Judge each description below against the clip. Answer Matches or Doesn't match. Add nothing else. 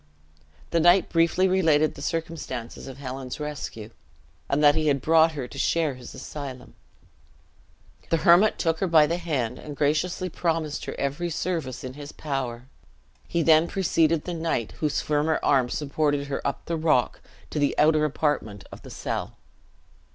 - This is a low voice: Doesn't match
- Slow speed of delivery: Doesn't match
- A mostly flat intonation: Doesn't match